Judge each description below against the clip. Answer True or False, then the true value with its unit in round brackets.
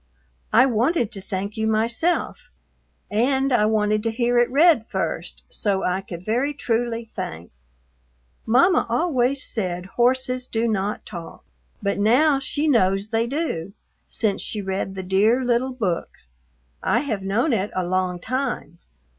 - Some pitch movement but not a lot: True (4.6 semitones)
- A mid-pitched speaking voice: False (225 Hz)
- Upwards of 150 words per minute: False (145 wpm)